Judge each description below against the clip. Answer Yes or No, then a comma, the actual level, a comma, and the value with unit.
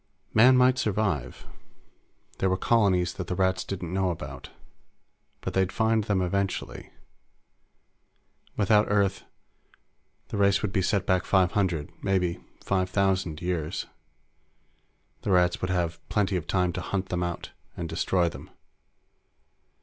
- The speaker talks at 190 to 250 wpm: No, average, 140 wpm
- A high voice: No, very low, 95 Hz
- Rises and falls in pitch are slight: Yes, narrow, 2.1 semitones